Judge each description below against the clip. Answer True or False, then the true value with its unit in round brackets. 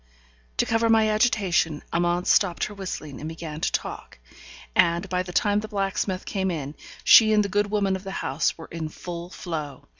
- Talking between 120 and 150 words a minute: False (190 wpm)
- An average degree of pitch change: True (3.8 semitones)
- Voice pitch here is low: False (185 Hz)